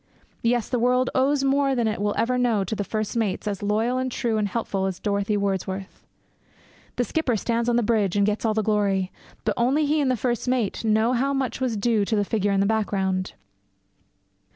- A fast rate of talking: Yes, fast, 210 wpm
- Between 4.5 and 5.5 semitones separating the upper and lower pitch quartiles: No, average, 3.5 semitones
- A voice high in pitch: Yes, high, 220 Hz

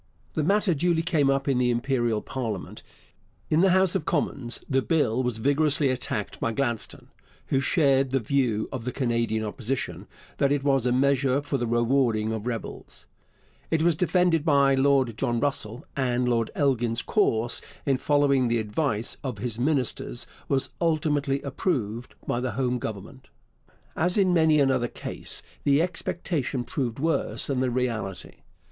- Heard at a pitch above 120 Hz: Yes, low, 135 Hz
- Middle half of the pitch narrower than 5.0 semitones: Yes, average, 3.5 semitones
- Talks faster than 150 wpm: Yes, average, 160 wpm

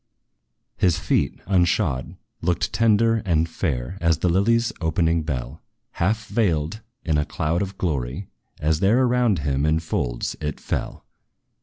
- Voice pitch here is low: Yes, very low, 85 Hz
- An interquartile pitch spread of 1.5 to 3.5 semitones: No, average, 4.8 semitones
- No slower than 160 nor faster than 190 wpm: No, average, 140 wpm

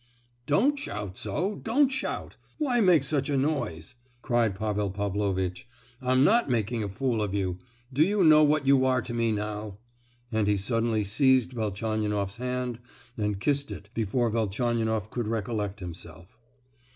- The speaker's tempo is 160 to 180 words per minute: No, average, 150 wpm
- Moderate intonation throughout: Yes, average, 4.8 semitones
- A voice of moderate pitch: No, low, 115 Hz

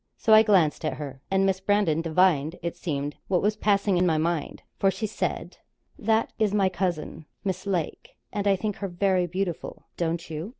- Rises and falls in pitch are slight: No, average, 3.4 semitones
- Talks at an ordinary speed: Yes, average, 195 wpm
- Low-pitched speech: No, medium, 185 Hz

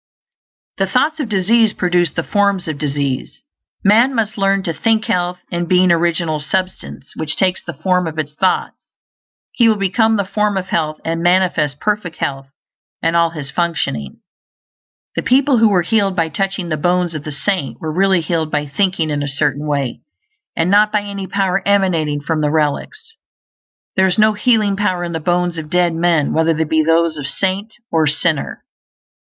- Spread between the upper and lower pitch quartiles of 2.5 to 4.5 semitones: Yes, average, 4.1 semitones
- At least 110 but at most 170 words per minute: No, average, 185 wpm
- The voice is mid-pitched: Yes, medium, 175 Hz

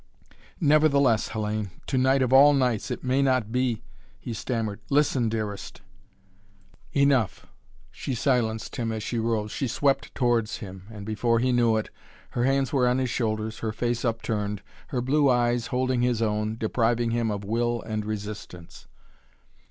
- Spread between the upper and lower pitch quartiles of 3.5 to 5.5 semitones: No, average, 3.0 semitones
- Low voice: Yes, low, 115 Hz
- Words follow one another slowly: No, average, 165 wpm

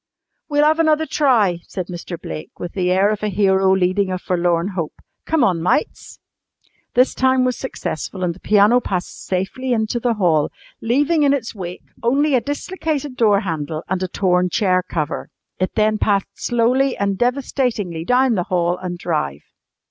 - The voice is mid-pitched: No, high, 200 Hz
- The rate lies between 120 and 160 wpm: No, average, 170 wpm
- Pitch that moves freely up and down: Yes, wide, 5.8 semitones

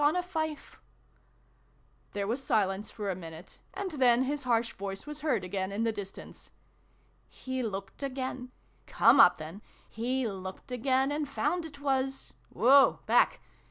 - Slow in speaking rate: No, average, 150 wpm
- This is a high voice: Yes, very high, 250 Hz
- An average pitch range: No, wide, 5.9 semitones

